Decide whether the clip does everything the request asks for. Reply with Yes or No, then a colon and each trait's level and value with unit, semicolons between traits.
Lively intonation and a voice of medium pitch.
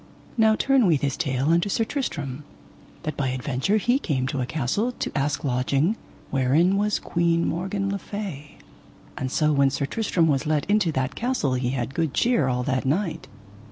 Yes: wide, 6.8 semitones; medium, 155 Hz